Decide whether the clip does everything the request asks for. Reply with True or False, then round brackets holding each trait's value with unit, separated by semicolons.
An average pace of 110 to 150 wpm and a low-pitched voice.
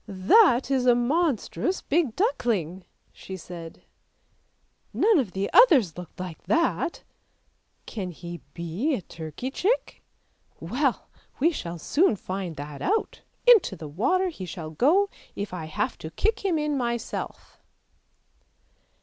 False (140 wpm; 230 Hz)